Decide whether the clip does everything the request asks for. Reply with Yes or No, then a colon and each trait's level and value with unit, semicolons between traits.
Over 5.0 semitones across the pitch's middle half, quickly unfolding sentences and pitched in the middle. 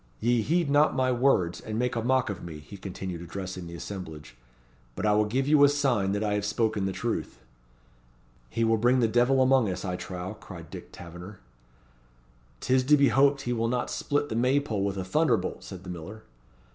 No: wide, 5.5 semitones; fast, 210 wpm; low, 110 Hz